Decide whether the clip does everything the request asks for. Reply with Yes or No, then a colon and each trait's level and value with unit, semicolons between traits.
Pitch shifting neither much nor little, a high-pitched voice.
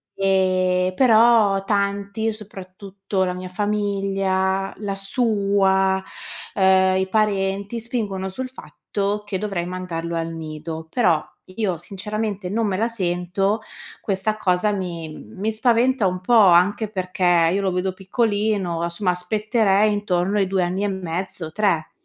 No: narrow, 2.3 semitones; high, 195 Hz